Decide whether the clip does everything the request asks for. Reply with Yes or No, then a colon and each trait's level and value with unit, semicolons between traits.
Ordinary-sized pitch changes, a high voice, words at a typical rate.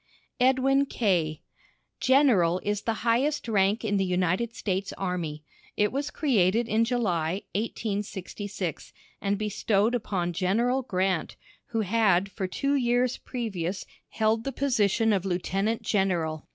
No: average, 4.2 semitones; high, 205 Hz; slow, 125 wpm